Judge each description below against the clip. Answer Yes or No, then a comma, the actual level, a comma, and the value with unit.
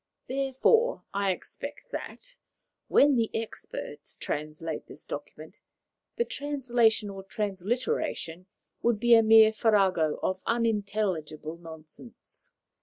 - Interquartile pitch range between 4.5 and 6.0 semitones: Yes, average, 4.9 semitones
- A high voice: Yes, high, 215 Hz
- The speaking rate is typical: No, slow, 105 wpm